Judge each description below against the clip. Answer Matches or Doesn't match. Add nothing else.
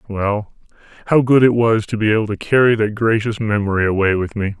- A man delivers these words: Matches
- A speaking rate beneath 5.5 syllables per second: Doesn't match